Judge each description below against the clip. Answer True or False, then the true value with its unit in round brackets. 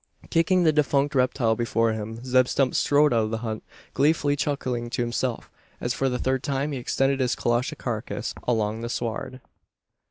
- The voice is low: True (125 Hz)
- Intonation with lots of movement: False (2.9 semitones)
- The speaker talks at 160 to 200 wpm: True (180 wpm)